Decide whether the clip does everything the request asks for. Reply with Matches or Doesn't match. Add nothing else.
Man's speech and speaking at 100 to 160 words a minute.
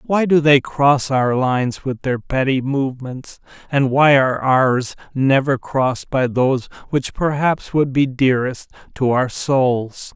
Matches